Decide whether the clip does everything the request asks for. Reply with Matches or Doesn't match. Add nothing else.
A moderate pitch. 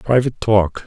Doesn't match